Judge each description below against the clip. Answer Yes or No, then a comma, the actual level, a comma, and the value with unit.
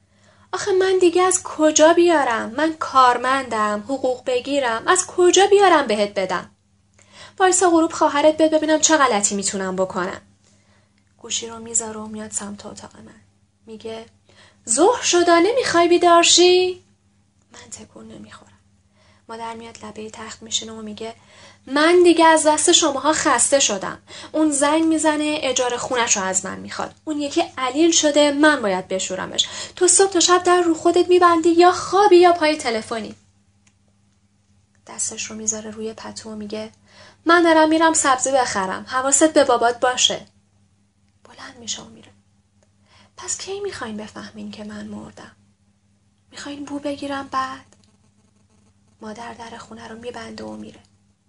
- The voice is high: Yes, high, 225 Hz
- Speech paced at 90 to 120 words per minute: No, average, 140 wpm